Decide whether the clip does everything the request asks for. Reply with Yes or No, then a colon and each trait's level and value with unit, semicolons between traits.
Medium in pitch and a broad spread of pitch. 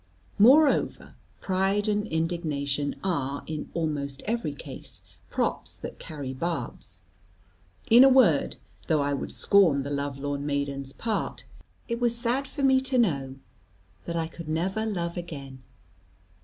Yes: medium, 160 Hz; wide, 6.9 semitones